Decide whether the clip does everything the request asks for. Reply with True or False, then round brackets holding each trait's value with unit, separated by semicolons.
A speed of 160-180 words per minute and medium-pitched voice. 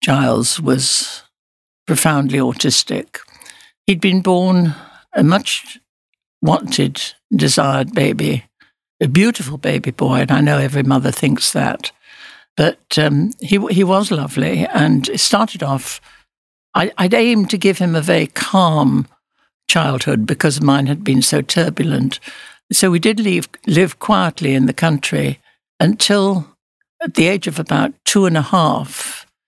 False (140 wpm; 165 Hz)